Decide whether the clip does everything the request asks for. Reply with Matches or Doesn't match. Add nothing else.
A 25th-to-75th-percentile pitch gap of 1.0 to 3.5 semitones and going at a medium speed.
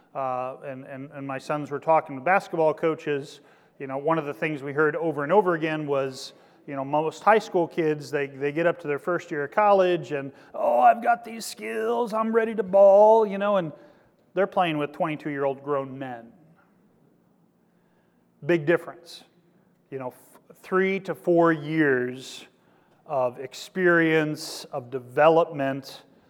Doesn't match